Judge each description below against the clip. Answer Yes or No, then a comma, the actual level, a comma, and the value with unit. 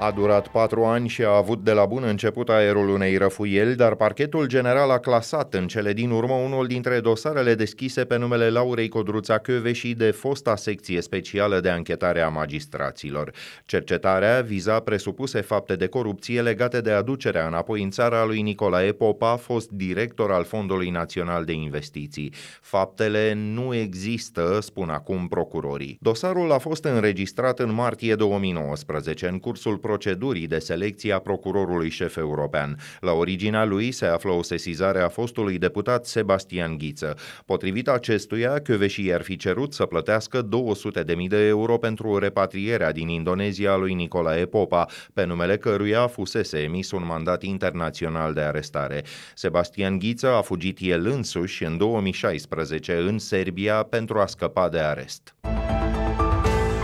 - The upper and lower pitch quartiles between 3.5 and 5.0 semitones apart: Yes, average, 4.2 semitones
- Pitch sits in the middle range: No, low, 105 Hz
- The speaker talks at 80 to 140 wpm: No, average, 150 wpm